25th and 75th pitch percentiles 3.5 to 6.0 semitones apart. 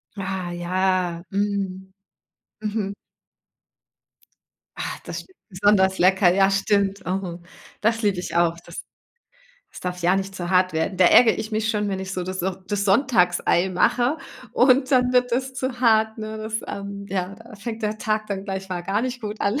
No: average, 2.7 semitones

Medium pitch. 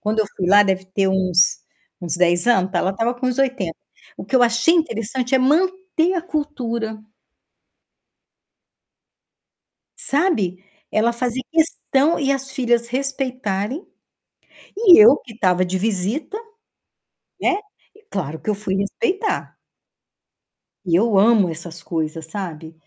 No: high, 225 Hz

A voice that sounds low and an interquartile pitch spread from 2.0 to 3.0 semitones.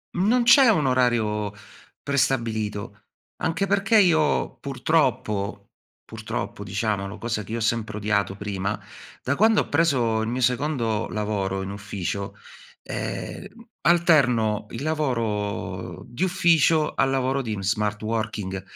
No: low, 115 Hz; wide, 6.4 semitones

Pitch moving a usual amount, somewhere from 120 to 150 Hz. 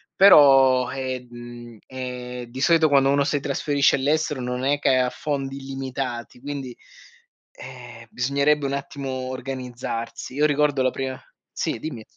No: narrow, 2.1 semitones; low, 135 Hz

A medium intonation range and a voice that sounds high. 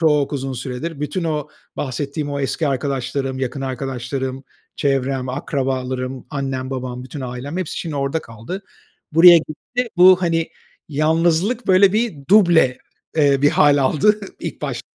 No: average, 3.8 semitones; medium, 140 Hz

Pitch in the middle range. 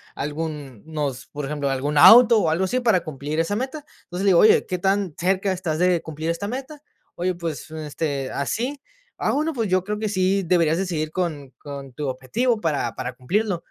Yes: medium, 170 Hz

